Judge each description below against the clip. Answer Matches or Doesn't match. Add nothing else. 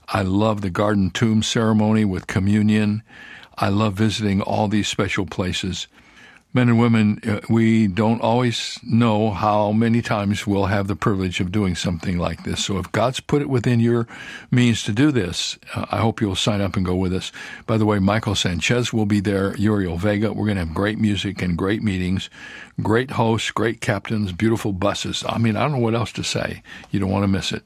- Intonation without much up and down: Matches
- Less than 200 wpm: Doesn't match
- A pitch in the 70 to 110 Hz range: Matches